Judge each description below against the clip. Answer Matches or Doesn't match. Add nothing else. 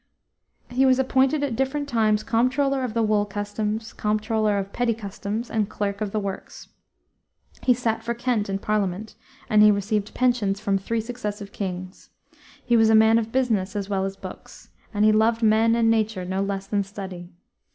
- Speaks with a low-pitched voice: Doesn't match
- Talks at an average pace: Matches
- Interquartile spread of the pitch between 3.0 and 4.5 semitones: Doesn't match